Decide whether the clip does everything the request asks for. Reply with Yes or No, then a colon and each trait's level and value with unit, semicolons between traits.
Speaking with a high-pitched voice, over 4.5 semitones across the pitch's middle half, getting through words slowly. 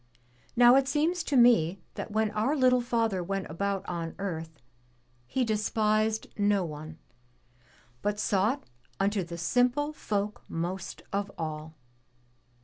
Yes: high, 205 Hz; wide, 5.4 semitones; slow, 130 wpm